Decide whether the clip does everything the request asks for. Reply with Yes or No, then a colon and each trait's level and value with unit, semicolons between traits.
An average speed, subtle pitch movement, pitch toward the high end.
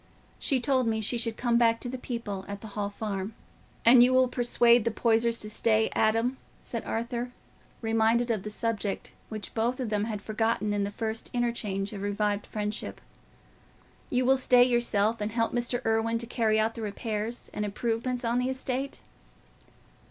Yes: average, 180 wpm; narrow, 2.2 semitones; high, 230 Hz